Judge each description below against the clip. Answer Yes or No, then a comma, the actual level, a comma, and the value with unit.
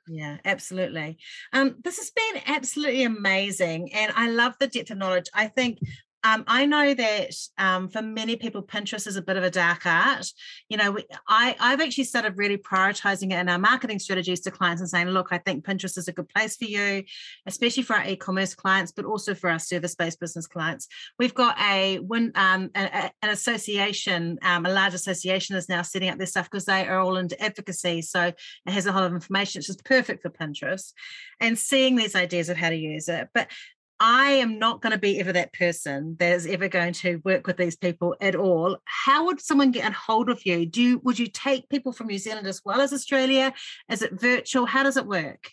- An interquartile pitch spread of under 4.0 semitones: No, average, 4.9 semitones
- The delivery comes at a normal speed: No, fast, 220 wpm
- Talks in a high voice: Yes, high, 195 Hz